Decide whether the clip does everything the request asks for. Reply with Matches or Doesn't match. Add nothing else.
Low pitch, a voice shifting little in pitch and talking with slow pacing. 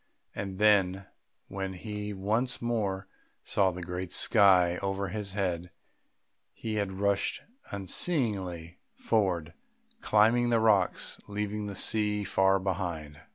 Matches